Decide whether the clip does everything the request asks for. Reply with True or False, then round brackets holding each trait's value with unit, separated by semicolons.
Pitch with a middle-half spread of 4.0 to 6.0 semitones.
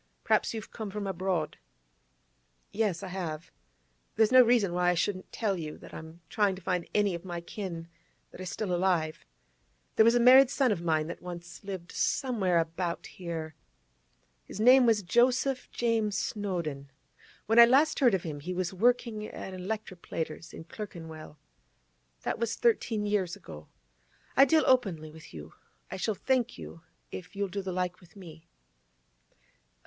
True (4.5 semitones)